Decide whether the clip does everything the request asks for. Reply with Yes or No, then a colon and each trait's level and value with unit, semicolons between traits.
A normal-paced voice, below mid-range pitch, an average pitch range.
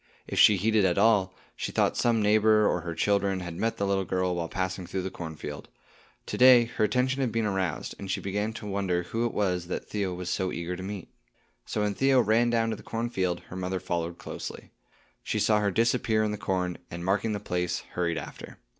No: fast, 220 wpm; low, 100 Hz; average, 3.3 semitones